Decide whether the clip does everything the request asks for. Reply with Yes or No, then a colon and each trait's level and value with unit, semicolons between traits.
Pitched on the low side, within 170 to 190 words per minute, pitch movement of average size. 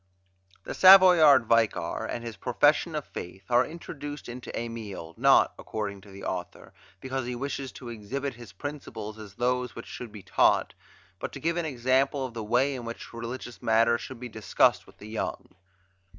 Yes: low, 120 Hz; average, 180 wpm; average, 3.5 semitones